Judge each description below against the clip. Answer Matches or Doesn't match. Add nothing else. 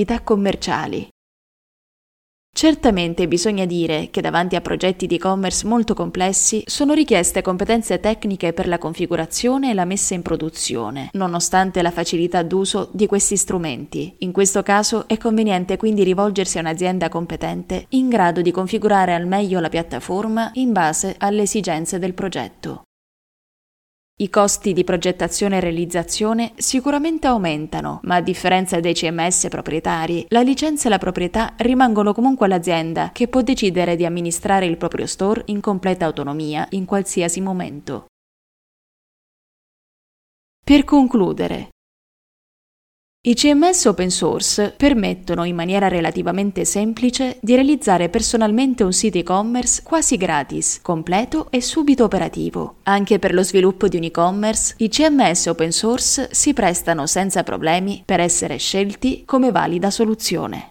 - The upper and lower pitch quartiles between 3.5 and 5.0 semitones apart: Matches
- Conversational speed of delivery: Matches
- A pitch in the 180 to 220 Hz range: Matches